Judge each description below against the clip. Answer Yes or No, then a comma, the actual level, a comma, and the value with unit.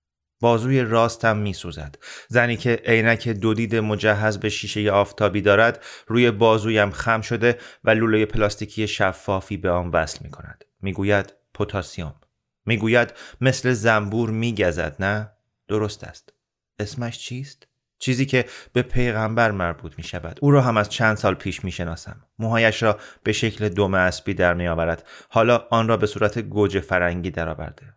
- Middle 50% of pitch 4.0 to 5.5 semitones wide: No, average, 3.0 semitones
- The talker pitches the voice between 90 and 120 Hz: Yes, low, 105 Hz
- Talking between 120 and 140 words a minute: No, fast, 155 wpm